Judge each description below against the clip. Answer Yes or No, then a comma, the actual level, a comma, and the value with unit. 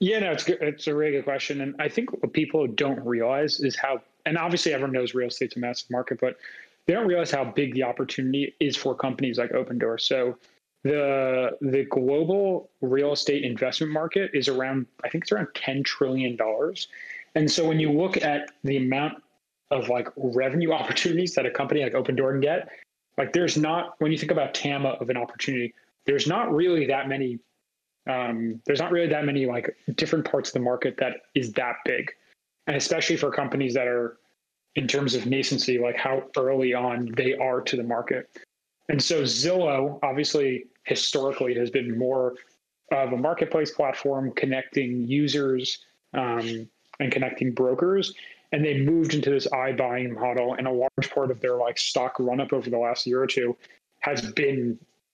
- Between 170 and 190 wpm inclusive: Yes, average, 185 wpm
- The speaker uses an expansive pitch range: No, average, 2.9 semitones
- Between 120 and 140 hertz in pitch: Yes, low, 135 Hz